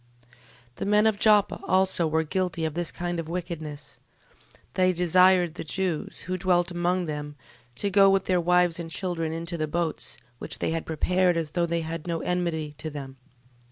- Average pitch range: No, narrow, 2.3 semitones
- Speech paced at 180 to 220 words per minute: Yes, average, 190 wpm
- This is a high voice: No, medium, 175 Hz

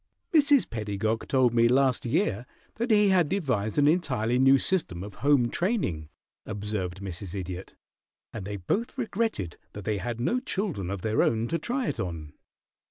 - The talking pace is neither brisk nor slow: Yes, average, 165 wpm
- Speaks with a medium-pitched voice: No, low, 115 Hz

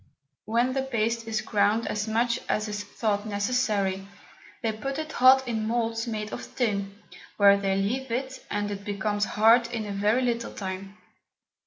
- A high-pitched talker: Yes, high, 220 Hz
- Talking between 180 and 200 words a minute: No, average, 170 wpm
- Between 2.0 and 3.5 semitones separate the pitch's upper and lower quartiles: Yes, narrow, 2.6 semitones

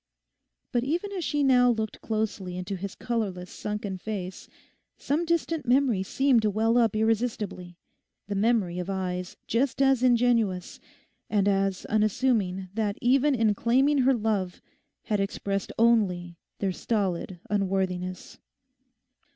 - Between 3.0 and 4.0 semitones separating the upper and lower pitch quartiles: No, average, 4.4 semitones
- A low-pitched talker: No, high, 215 Hz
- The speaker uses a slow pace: Yes, slow, 125 wpm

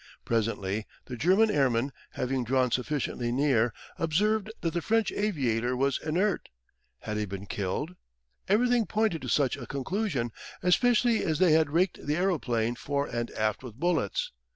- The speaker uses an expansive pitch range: Yes, wide, 7.5 semitones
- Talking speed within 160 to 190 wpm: No, average, 150 wpm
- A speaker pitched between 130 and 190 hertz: Yes, medium, 140 Hz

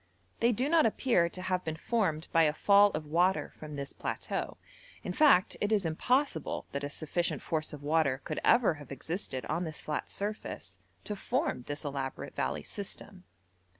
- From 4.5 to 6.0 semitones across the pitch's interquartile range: Yes, wide, 5.5 semitones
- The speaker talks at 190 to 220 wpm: No, average, 180 wpm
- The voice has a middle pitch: Yes, medium, 165 Hz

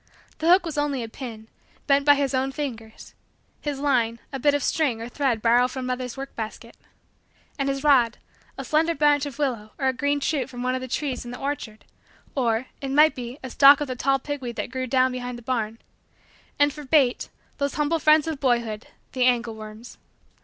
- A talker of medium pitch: No, very high, 260 Hz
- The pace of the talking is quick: Yes, fast, 210 wpm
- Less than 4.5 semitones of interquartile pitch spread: Yes, average, 3.0 semitones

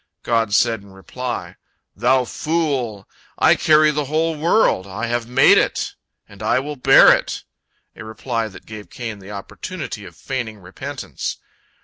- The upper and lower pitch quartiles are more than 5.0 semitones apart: Yes, wide, 5.4 semitones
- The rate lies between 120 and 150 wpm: Yes, average, 145 wpm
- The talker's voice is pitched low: Yes, low, 120 Hz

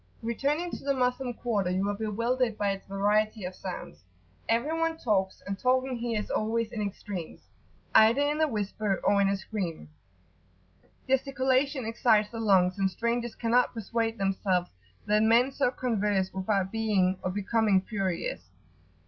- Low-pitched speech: No, high, 220 Hz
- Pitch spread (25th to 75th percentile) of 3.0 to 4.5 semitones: Yes, average, 3.8 semitones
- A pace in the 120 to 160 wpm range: Yes, average, 155 wpm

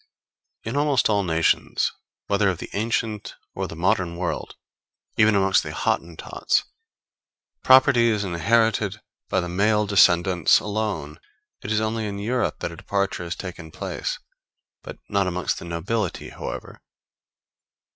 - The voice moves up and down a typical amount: Yes, average, 3.9 semitones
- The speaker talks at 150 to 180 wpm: No, slow, 135 wpm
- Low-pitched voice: Yes, low, 100 Hz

